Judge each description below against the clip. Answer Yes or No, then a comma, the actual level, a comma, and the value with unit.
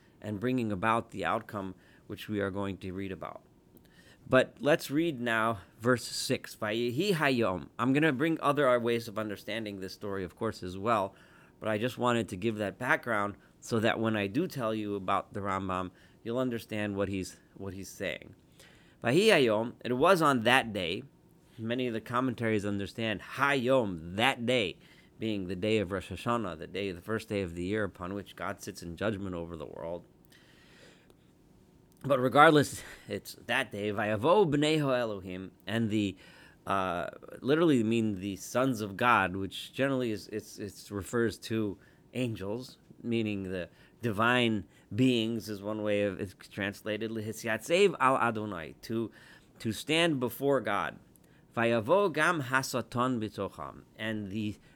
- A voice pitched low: Yes, low, 110 Hz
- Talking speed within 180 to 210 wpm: No, average, 155 wpm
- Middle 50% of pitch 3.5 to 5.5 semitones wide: Yes, average, 3.8 semitones